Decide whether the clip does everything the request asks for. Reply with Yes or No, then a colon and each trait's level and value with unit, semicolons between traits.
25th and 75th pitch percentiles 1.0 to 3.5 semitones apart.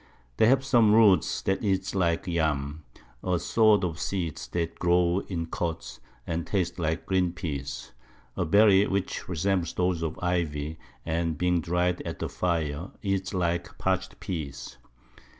Yes: narrow, 2.6 semitones